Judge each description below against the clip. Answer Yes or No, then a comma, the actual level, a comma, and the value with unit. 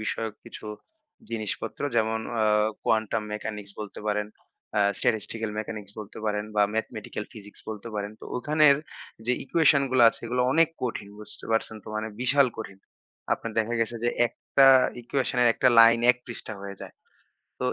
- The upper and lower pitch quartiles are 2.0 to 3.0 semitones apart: Yes, narrow, 2.5 semitones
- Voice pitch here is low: Yes, low, 110 Hz